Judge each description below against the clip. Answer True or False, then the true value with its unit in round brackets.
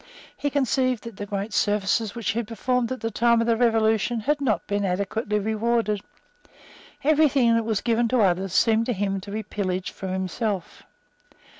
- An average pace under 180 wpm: False (185 wpm)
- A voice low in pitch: False (220 Hz)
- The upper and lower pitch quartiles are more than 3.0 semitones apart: False (2.7 semitones)